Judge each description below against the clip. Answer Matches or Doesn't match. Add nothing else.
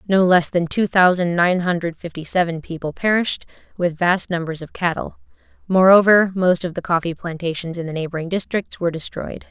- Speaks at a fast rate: Doesn't match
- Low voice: Doesn't match